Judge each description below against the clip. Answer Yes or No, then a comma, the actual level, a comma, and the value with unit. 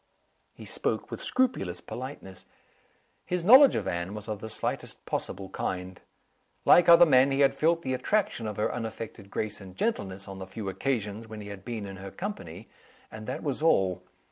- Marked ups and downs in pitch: Yes, wide, 6.3 semitones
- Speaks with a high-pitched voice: No, low, 110 Hz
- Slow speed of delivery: No, average, 185 wpm